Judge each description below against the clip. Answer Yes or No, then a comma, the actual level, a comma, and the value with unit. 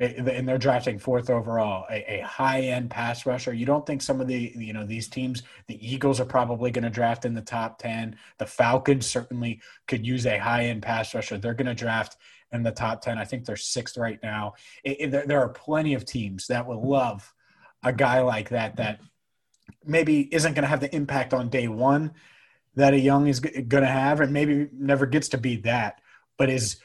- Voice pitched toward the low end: Yes, low, 125 Hz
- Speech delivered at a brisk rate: Yes, fast, 215 wpm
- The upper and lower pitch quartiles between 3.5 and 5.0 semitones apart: No, average, 3.0 semitones